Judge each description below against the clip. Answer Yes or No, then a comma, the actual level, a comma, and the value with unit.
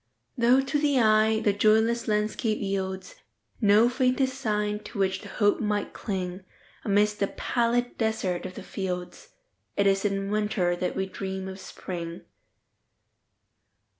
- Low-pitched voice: No, high, 210 Hz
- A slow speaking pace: Yes, slow, 130 wpm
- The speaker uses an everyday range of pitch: Yes, average, 3.4 semitones